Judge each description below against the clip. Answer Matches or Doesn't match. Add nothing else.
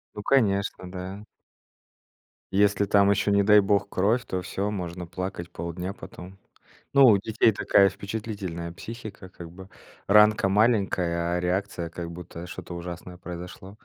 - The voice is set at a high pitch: Doesn't match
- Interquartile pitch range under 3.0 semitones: Matches